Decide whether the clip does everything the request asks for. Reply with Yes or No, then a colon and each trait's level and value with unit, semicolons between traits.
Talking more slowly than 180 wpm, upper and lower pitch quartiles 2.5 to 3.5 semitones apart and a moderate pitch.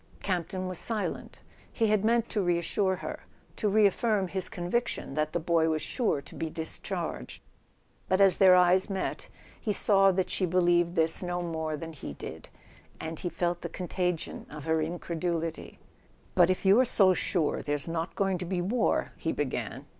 No: average, 185 wpm; average, 2.8 semitones; medium, 180 Hz